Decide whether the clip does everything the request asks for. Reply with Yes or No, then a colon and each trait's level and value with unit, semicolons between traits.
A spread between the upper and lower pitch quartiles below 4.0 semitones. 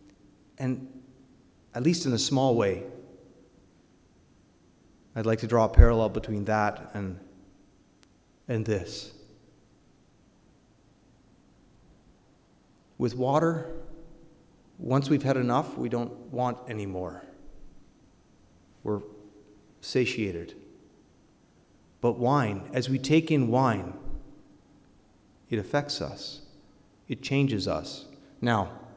No: average, 4.8 semitones